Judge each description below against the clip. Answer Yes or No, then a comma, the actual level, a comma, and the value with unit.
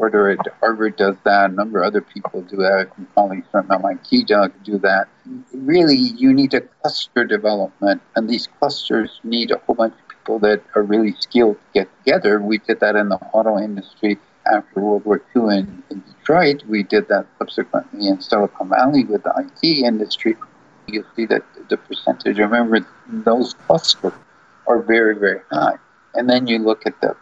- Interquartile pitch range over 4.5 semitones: Yes, average, 5.2 semitones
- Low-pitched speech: Yes, low, 110 Hz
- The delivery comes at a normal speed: Yes, average, 180 wpm